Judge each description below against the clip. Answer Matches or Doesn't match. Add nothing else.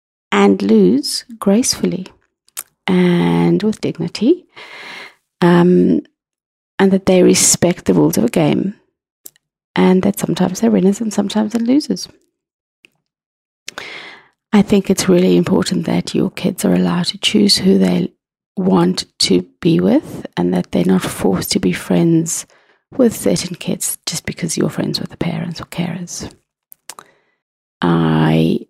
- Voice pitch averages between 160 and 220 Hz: Matches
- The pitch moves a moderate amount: Matches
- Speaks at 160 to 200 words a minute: Doesn't match